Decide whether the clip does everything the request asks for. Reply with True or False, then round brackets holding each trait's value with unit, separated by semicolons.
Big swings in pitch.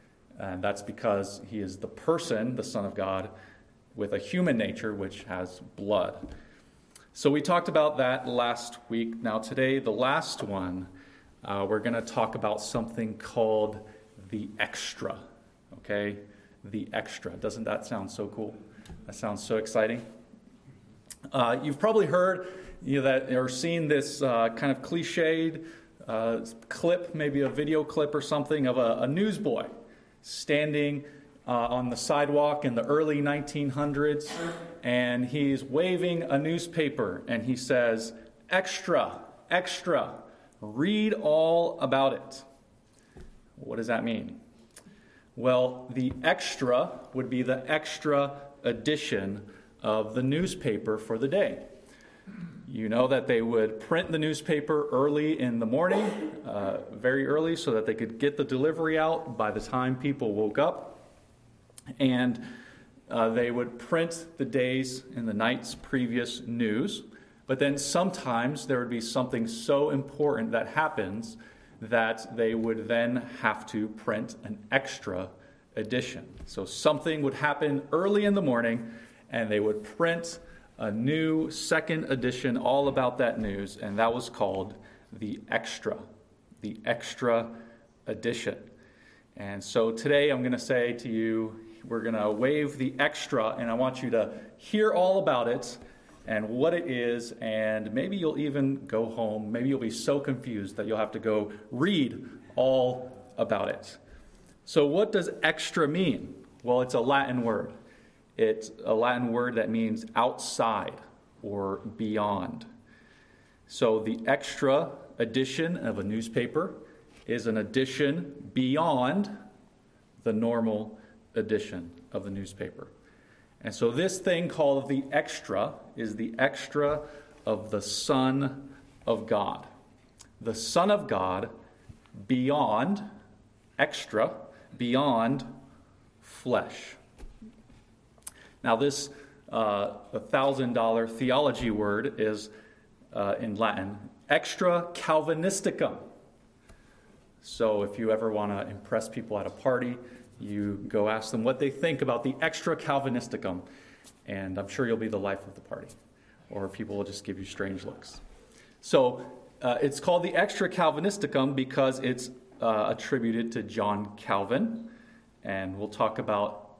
False (4.8 semitones)